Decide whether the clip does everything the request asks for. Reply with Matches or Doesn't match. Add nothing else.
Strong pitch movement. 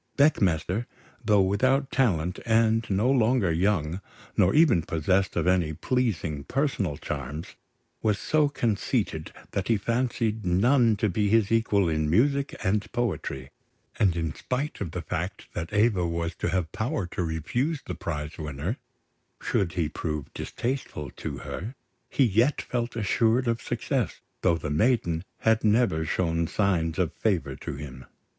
Matches